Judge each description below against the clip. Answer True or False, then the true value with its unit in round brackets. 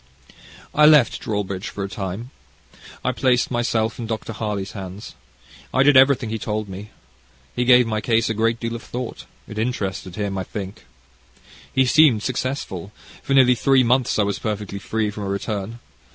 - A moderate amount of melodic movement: True (3.5 semitones)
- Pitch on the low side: True (110 Hz)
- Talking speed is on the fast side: False (175 wpm)